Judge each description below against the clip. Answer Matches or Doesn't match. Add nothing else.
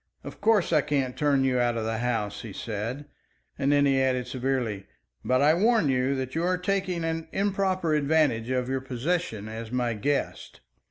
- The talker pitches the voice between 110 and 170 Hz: Matches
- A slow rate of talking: Doesn't match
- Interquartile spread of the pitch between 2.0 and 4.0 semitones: Doesn't match